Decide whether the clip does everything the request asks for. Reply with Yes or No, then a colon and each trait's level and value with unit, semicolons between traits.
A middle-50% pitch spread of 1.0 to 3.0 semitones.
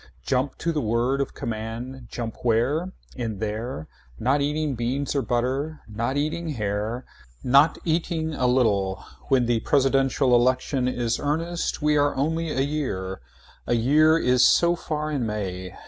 No: average, 4.2 semitones